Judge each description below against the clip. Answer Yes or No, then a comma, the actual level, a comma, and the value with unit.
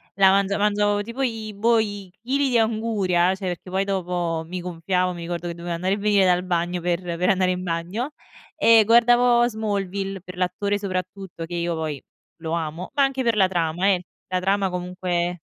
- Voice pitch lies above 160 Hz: Yes, medium, 185 Hz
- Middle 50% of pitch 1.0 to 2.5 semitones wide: No, average, 2.9 semitones